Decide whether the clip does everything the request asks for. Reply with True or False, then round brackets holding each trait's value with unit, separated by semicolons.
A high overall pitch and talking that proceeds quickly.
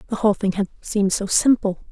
True (205 Hz; 220 wpm)